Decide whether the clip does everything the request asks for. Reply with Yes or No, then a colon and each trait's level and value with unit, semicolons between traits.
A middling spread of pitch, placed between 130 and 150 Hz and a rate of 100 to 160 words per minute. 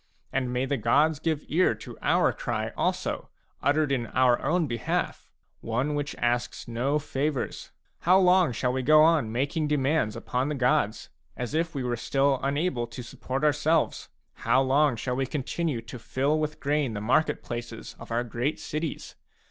No: average, 3.7 semitones; low, 135 Hz; average, 175 wpm